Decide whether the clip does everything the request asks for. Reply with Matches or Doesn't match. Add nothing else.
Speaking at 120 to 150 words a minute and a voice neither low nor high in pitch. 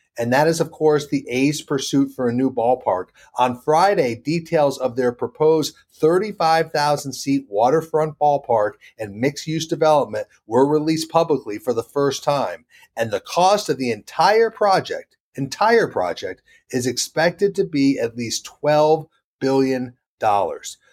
Matches